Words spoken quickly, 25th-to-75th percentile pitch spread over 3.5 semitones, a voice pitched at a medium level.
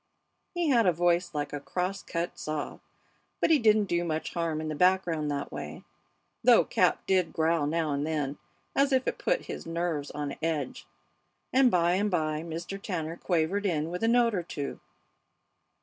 No: average, 180 wpm; average, 3.9 semitones; medium, 170 Hz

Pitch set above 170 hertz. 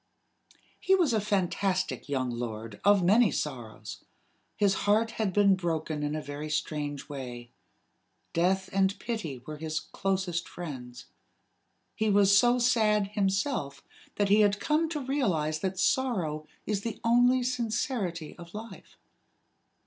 Yes: high, 190 Hz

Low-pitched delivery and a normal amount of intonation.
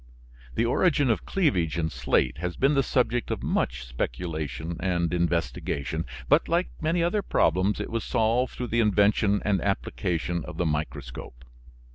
No: very low, 95 Hz; wide, 7.3 semitones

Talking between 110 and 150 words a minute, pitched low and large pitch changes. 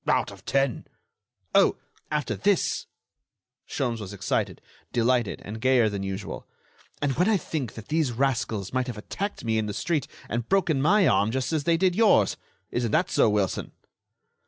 No: average, 170 wpm; low, 130 Hz; wide, 6.4 semitones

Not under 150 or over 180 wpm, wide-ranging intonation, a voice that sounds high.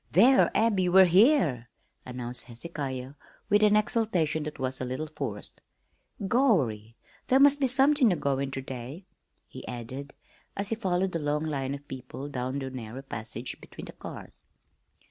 No: average, 160 wpm; wide, 7.9 semitones; medium, 145 Hz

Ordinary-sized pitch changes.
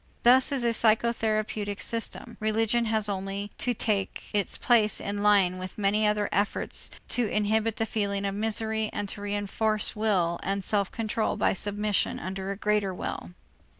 No: narrow, 1.7 semitones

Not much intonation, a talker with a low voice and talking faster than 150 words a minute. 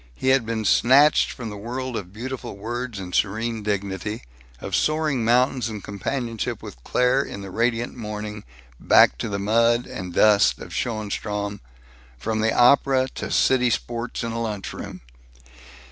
No: average, 3.1 semitones; low, 115 Hz; average, 160 wpm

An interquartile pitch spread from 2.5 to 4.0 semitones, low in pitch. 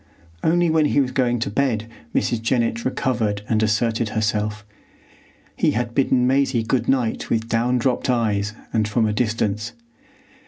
Yes: average, 2.8 semitones; low, 115 Hz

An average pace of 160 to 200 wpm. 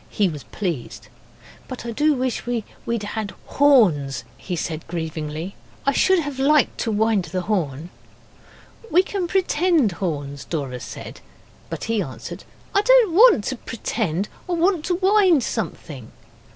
No: average, 145 wpm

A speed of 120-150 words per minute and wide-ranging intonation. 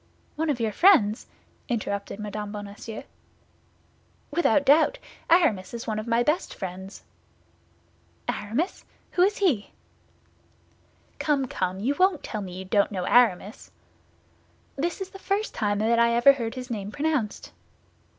Yes: slow, 135 wpm; wide, 6.6 semitones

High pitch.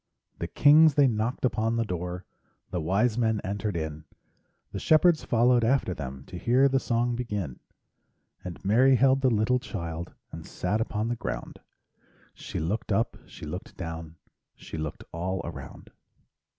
No: low, 110 Hz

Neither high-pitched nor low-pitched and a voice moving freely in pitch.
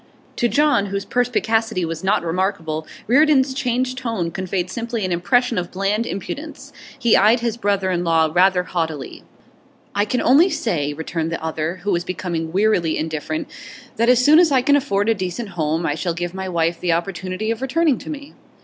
No: high, 195 Hz; wide, 6.0 semitones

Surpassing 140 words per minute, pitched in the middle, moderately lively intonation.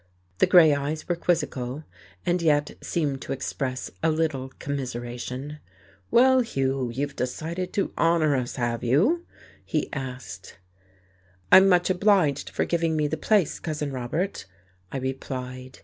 No: slow, 135 wpm; medium, 145 Hz; average, 4.8 semitones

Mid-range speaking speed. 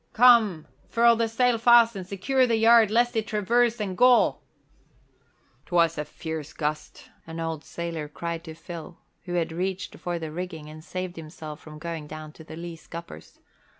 Yes: average, 175 wpm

